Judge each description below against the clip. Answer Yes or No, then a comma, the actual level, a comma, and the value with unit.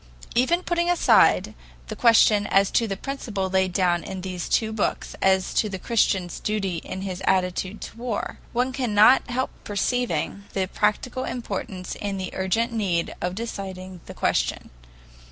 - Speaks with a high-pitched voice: Yes, high, 200 Hz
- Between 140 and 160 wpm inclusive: Yes, average, 155 wpm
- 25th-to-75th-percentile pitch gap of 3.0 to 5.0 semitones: Yes, average, 3.9 semitones